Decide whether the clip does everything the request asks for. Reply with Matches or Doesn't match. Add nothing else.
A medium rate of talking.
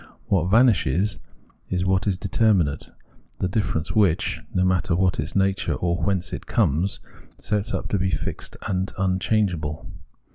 Matches